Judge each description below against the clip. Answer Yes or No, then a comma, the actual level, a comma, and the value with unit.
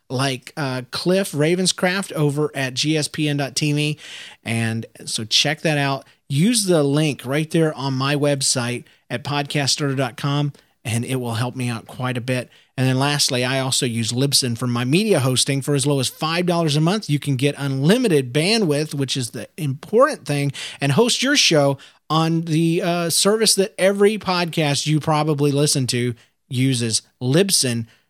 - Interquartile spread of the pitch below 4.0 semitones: Yes, average, 3.4 semitones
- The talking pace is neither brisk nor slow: Yes, average, 160 wpm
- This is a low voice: No, medium, 145 Hz